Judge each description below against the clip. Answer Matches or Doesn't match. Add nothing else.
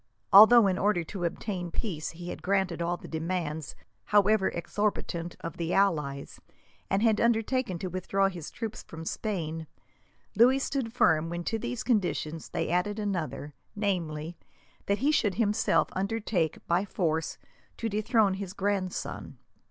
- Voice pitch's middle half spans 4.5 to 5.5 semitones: Doesn't match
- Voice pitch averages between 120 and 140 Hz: Doesn't match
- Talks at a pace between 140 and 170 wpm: Matches